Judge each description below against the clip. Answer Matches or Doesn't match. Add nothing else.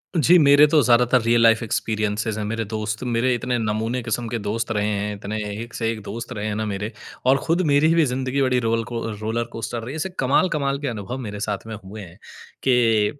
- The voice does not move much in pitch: Doesn't match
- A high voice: Doesn't match